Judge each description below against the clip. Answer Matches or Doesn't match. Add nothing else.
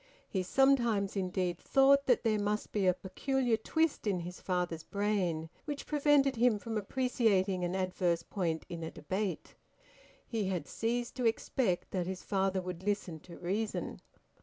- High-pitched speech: Matches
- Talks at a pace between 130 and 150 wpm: Doesn't match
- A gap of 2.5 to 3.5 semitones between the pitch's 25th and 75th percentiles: Doesn't match